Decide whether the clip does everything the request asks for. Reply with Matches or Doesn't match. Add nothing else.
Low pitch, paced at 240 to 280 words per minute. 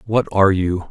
Doesn't match